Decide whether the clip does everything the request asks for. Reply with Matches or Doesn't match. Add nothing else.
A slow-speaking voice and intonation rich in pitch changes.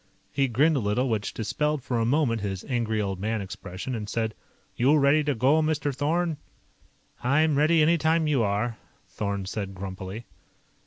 Doesn't match